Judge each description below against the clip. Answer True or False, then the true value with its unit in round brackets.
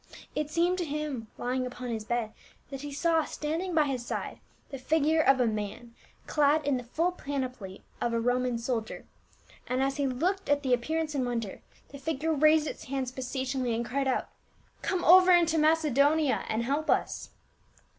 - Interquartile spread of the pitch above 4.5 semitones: False (4.0 semitones)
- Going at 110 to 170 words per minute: False (185 wpm)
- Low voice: False (275 Hz)